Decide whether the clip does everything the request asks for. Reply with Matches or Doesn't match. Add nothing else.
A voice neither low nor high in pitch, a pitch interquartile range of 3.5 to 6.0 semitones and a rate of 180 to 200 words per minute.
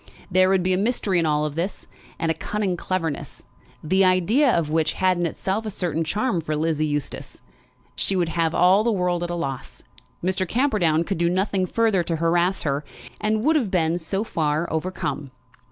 Doesn't match